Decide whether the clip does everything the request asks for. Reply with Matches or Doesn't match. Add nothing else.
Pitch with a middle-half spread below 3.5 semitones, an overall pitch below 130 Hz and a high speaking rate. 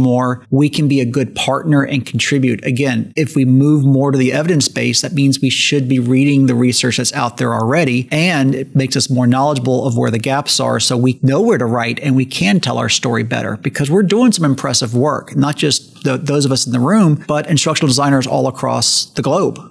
Doesn't match